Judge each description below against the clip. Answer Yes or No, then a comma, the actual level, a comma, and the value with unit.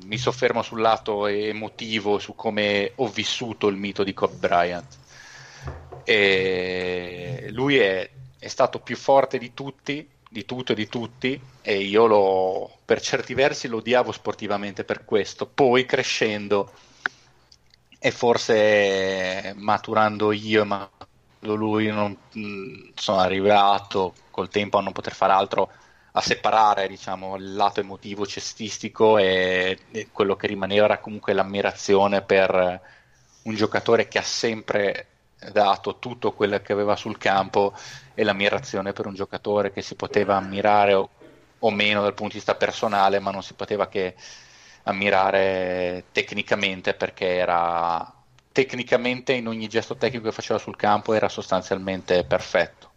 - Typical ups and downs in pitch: No, narrow, 2.3 semitones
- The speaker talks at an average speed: Yes, average, 135 wpm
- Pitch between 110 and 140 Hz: No, low, 100 Hz